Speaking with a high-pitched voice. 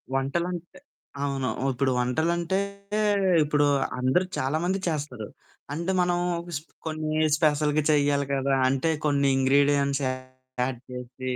No: medium, 140 Hz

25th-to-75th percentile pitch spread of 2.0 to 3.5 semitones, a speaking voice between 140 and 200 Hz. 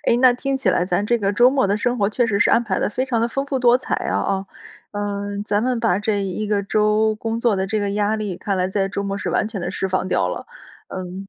No: average, 3.0 semitones; high, 210 Hz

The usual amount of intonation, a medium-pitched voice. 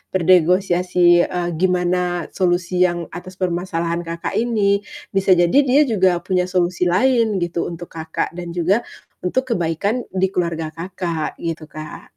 No: narrow, 1.7 semitones; medium, 180 Hz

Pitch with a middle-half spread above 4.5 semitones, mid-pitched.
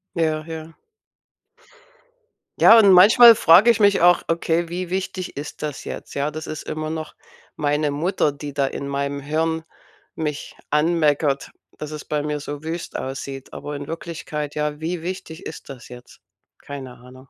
No: average, 2.7 semitones; medium, 155 Hz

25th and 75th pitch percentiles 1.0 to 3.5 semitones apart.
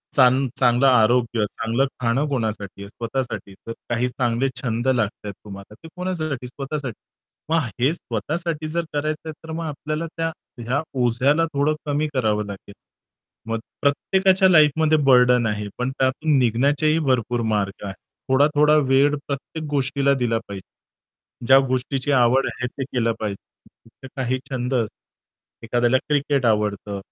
No: average, 4.1 semitones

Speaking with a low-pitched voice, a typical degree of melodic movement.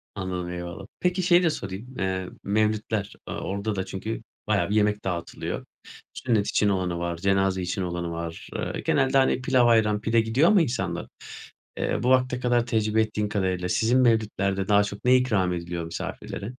Yes: low, 105 Hz; average, 4.2 semitones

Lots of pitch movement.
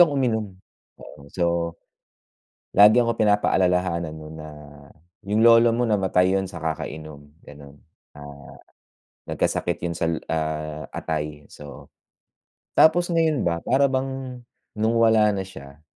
Yes: wide, 6.9 semitones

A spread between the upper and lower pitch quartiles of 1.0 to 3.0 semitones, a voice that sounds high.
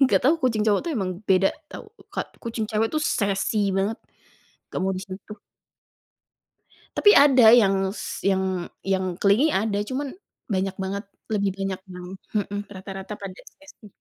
Yes: narrow, 2.6 semitones; high, 200 Hz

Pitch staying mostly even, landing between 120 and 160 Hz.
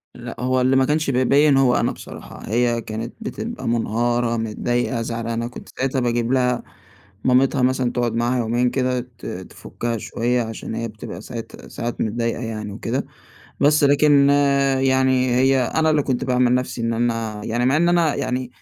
Yes: narrow, 2.1 semitones; low, 125 Hz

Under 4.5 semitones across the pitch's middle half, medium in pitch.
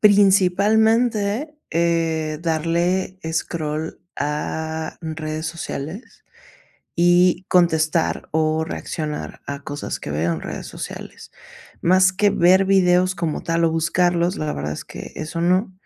Yes: average, 3.0 semitones; medium, 170 Hz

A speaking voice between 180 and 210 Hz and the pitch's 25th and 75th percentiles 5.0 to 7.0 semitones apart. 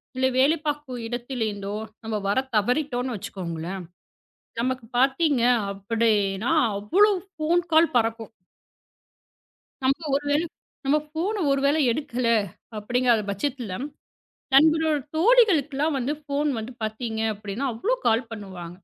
No: very high, 255 Hz; average, 5.3 semitones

